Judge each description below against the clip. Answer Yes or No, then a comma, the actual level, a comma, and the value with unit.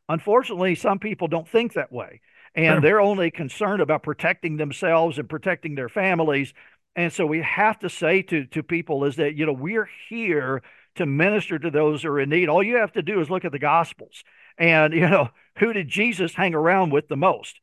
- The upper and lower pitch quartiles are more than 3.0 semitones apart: Yes, average, 3.7 semitones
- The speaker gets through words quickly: Yes, fast, 210 wpm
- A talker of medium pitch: Yes, medium, 165 Hz